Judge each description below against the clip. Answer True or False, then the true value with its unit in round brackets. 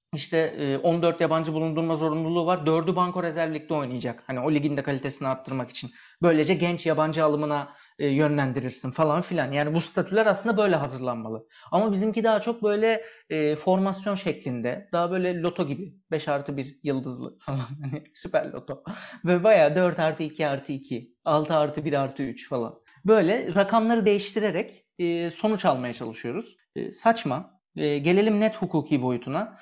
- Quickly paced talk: True (145 wpm)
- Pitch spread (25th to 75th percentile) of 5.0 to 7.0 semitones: False (4.6 semitones)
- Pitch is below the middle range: False (160 Hz)